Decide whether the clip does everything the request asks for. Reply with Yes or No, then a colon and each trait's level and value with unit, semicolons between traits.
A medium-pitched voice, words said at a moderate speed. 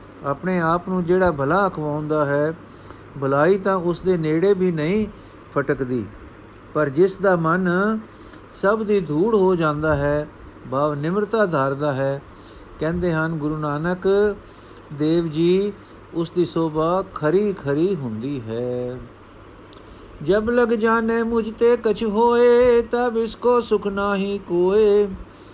Yes: medium, 170 Hz; average, 125 wpm